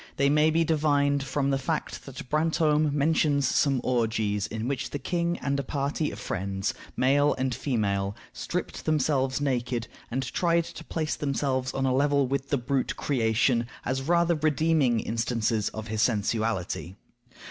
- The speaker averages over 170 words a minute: No, average, 160 wpm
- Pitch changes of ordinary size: Yes, average, 4.0 semitones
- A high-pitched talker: No, low, 135 Hz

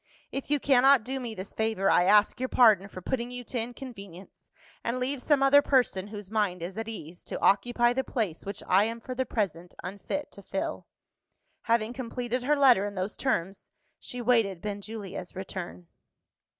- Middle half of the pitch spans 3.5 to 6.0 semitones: Yes, average, 4.3 semitones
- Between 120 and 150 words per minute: No, average, 180 wpm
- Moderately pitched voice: No, high, 225 Hz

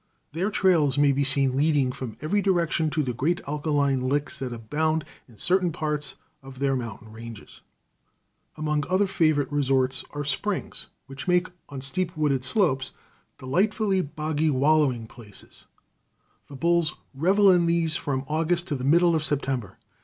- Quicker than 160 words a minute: No, average, 155 wpm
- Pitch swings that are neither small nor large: Yes, average, 4.0 semitones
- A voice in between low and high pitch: Yes, medium, 150 Hz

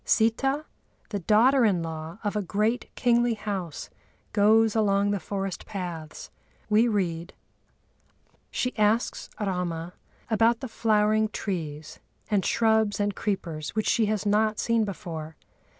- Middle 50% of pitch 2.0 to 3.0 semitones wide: No, average, 3.5 semitones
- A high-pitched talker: Yes, high, 210 Hz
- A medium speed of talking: No, slow, 130 wpm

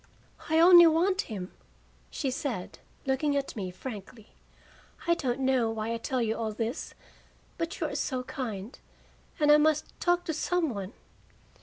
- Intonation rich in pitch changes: Yes, wide, 5.9 semitones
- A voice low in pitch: No, very high, 265 Hz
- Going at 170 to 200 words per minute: No, average, 160 wpm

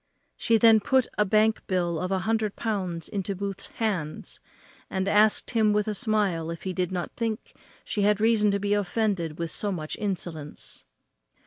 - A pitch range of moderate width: Yes, average, 3.1 semitones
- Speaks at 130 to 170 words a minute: No, average, 185 wpm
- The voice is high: Yes, high, 200 Hz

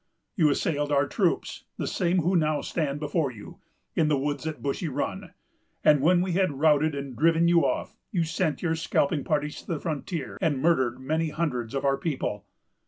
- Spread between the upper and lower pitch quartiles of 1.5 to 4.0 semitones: Yes, average, 2.9 semitones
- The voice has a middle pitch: Yes, medium, 150 Hz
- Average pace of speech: Yes, average, 180 wpm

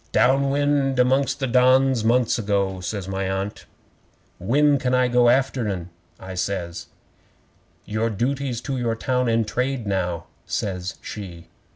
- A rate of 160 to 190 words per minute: No, average, 145 wpm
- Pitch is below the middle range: Yes, low, 115 Hz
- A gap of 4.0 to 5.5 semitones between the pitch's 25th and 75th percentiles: Yes, average, 5.2 semitones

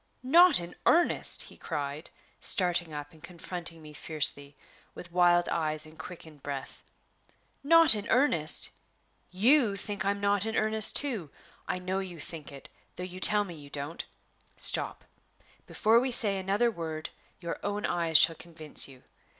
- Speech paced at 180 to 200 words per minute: No, average, 155 wpm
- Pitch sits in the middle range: Yes, medium, 175 Hz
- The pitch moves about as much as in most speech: Yes, average, 4.7 semitones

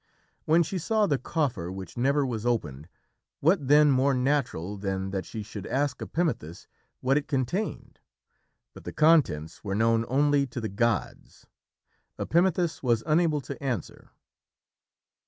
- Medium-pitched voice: No, low, 130 Hz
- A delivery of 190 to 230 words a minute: No, average, 140 wpm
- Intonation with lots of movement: Yes, wide, 6.0 semitones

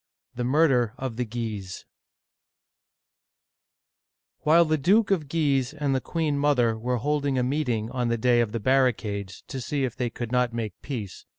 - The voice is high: No, low, 125 Hz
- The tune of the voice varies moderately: Yes, average, 3.7 semitones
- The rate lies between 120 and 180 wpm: Yes, average, 175 wpm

